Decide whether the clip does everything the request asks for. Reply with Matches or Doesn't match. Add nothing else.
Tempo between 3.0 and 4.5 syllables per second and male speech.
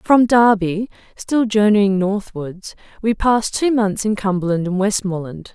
Doesn't match